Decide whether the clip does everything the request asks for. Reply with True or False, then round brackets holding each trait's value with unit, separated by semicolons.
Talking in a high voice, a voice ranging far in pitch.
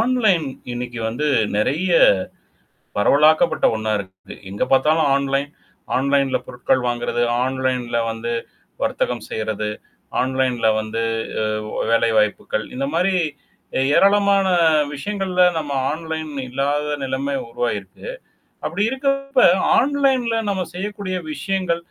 False (140 Hz; 7.7 semitones)